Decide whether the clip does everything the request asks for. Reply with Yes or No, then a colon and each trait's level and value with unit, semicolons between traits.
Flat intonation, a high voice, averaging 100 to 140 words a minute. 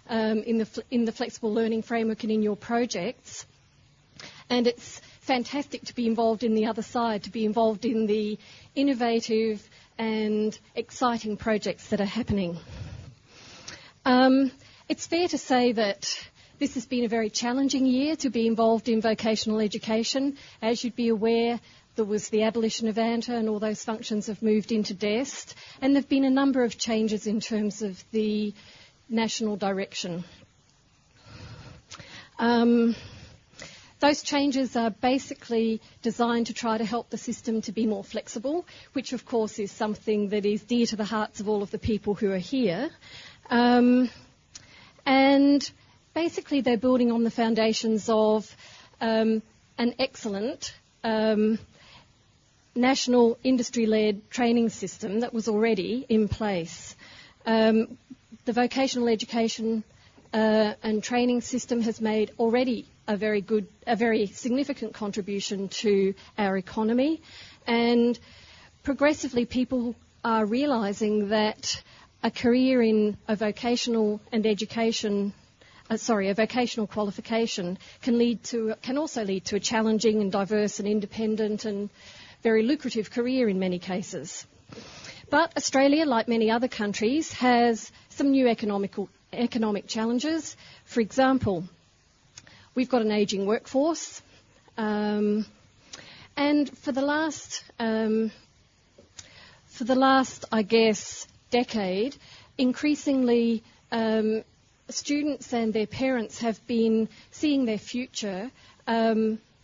Yes: narrow, 2.3 semitones; high, 225 Hz; slow, 135 wpm